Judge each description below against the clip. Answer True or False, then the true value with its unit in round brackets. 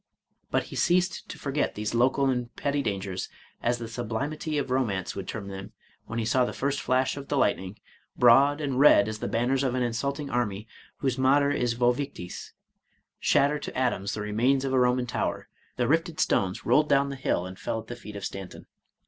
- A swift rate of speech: True (210 wpm)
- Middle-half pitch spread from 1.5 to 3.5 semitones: False (4.1 semitones)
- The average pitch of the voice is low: True (125 Hz)